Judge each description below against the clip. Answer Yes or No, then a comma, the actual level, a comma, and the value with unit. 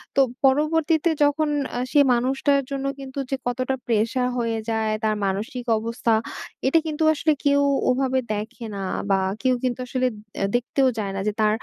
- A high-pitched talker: Yes, very high, 255 Hz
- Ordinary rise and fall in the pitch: Yes, average, 3.5 semitones